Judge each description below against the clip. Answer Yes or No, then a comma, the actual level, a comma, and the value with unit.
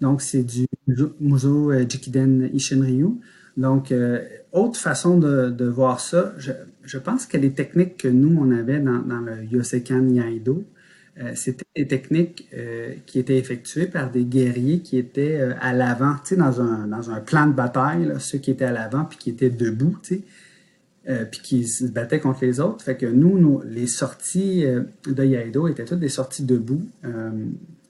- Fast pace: No, average, 185 wpm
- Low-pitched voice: Yes, low, 130 Hz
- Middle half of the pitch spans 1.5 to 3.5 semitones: Yes, average, 3.2 semitones